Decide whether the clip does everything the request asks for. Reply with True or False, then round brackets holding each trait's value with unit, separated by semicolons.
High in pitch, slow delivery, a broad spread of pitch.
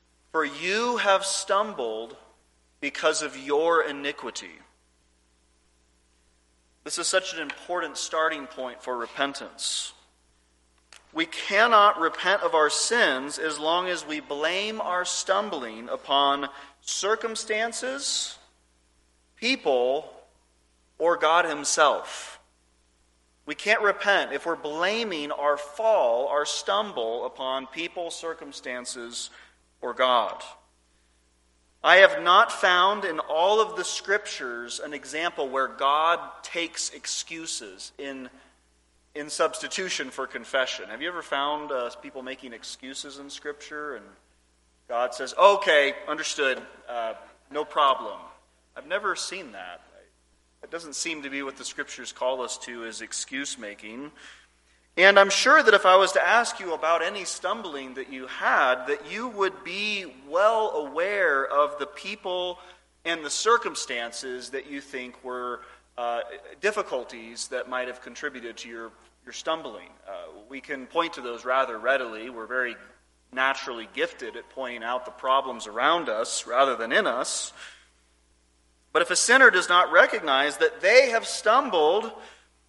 False (140 Hz; 130 wpm; 7.4 semitones)